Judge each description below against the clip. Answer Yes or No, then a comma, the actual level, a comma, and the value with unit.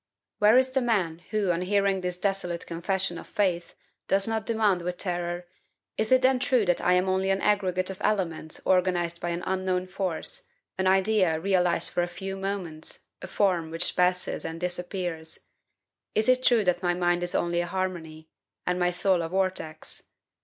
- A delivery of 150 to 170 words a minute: No, average, 180 wpm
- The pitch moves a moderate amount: No, narrow, 2.0 semitones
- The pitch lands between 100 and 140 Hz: No, medium, 185 Hz